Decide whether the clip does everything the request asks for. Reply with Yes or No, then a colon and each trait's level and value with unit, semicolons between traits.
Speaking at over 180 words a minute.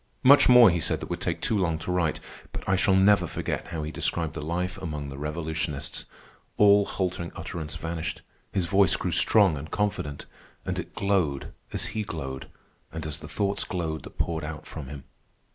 Yes: average, 195 wpm